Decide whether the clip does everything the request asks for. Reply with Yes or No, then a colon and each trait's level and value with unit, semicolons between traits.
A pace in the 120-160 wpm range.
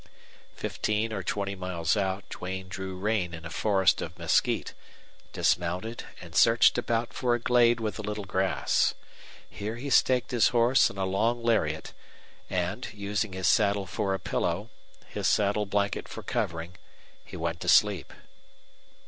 Yes: average, 155 wpm